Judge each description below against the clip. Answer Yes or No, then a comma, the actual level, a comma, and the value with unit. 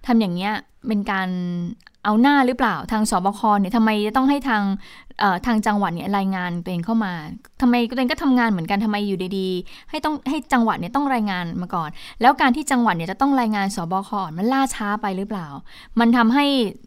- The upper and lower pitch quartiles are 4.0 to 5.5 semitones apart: Yes, average, 4.4 semitones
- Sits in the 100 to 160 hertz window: No, high, 210 Hz